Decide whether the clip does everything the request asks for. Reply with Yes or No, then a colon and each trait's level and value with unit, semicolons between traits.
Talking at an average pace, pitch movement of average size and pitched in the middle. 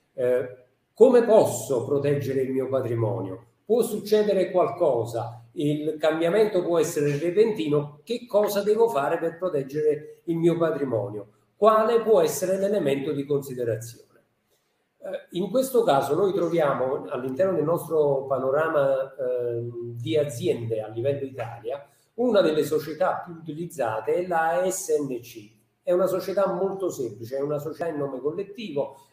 No: average, 135 wpm; wide, 6.2 semitones; medium, 155 Hz